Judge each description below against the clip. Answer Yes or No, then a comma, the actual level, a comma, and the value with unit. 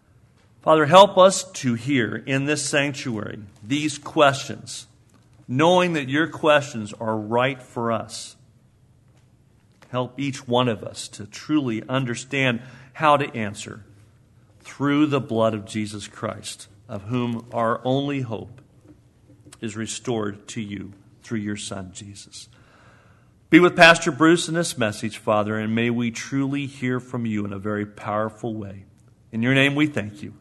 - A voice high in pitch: No, low, 120 Hz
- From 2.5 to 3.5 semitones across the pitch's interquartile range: No, average, 4.0 semitones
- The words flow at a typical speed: Yes, average, 145 wpm